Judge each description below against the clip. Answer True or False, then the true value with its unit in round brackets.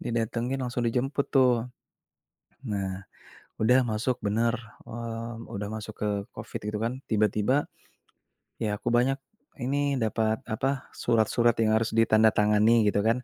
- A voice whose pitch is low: True (115 Hz)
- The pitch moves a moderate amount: False (1.9 semitones)